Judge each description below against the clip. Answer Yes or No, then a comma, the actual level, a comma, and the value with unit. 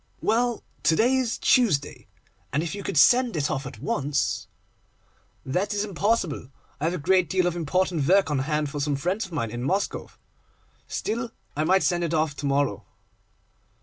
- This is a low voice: No, medium, 170 Hz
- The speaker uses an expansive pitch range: Yes, wide, 5.7 semitones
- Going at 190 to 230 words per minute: No, average, 180 wpm